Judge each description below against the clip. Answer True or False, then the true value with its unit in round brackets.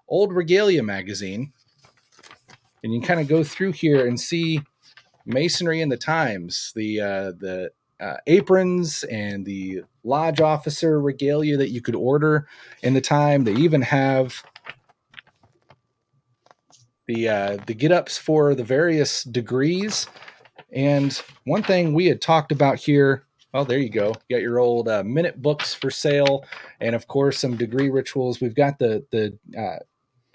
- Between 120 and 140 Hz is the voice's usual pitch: True (135 Hz)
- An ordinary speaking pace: True (155 wpm)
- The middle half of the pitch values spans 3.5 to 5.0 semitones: True (4.1 semitones)